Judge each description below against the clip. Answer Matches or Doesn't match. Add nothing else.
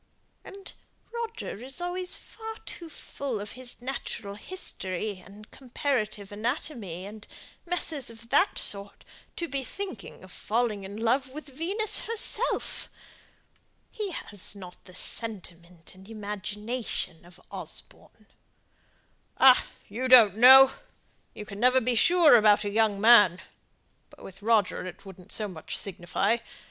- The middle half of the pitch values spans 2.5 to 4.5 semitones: Doesn't match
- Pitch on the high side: Matches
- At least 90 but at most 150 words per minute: Matches